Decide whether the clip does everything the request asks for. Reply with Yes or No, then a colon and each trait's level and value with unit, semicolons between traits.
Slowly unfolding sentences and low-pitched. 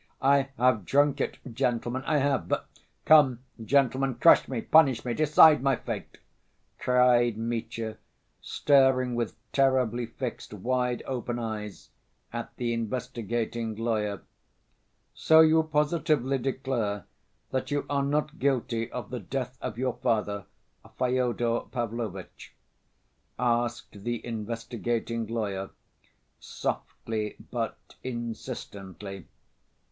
Yes: slow, 110 wpm; low, 120 Hz